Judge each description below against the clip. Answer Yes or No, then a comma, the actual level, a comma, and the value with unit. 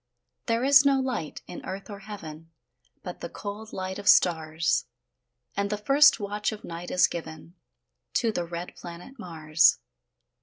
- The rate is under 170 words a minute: Yes, average, 155 wpm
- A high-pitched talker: Yes, high, 195 Hz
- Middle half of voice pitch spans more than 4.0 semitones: Yes, average, 4.6 semitones